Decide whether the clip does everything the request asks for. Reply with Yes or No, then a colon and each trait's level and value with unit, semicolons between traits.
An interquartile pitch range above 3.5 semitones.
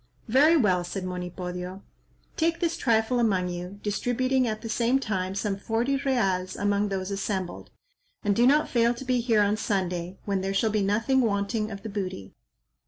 Yes: average, 4.0 semitones